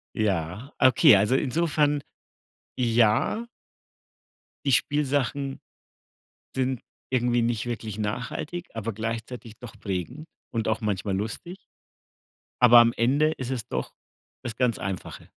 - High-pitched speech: No, low, 120 Hz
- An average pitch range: Yes, average, 3.7 semitones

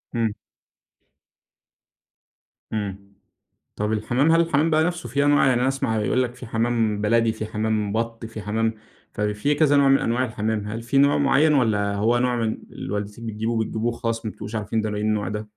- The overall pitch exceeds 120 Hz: No, low, 115 Hz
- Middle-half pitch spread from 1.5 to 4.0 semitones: Yes, average, 3.2 semitones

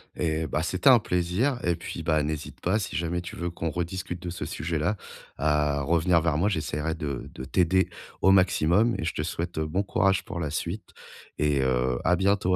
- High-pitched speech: No, very low, 85 Hz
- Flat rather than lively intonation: No, average, 3.3 semitones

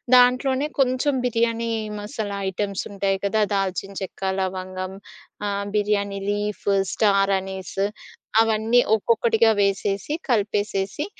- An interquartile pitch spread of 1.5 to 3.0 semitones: Yes, average, 2.7 semitones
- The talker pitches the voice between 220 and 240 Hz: No, high, 205 Hz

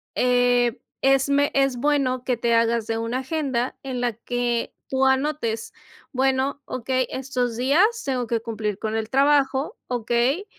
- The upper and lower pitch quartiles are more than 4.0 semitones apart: No, narrow, 2.4 semitones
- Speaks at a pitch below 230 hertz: No, very high, 255 Hz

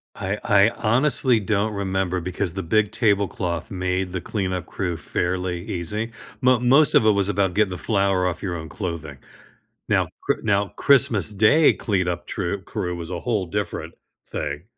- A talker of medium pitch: No, very low, 95 Hz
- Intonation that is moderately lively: Yes, average, 3.1 semitones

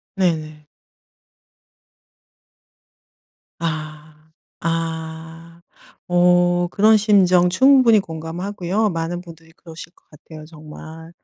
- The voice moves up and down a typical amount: No, narrow, 1.9 semitones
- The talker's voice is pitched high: No, medium, 165 Hz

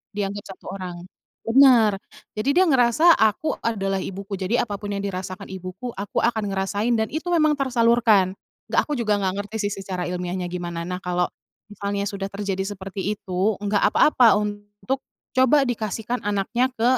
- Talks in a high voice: Yes, high, 205 Hz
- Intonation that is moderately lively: Yes, average, 3.5 semitones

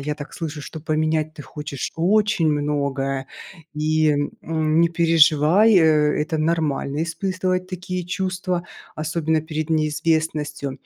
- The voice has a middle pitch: Yes, medium, 155 Hz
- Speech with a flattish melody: Yes, narrow, 2.1 semitones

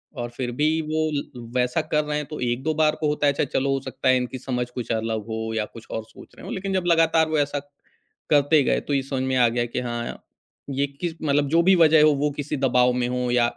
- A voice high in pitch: No, low, 135 Hz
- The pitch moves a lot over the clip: No, average, 3.8 semitones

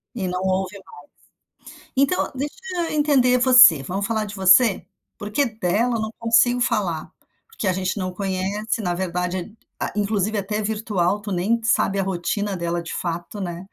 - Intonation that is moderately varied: Yes, average, 3.7 semitones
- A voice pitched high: Yes, high, 205 Hz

